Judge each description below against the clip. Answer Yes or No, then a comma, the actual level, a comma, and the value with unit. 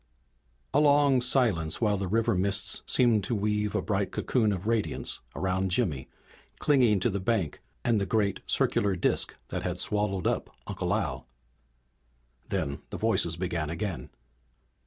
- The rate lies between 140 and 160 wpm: Yes, average, 150 wpm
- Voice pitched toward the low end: Yes, low, 100 Hz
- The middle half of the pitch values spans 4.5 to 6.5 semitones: No, average, 3.8 semitones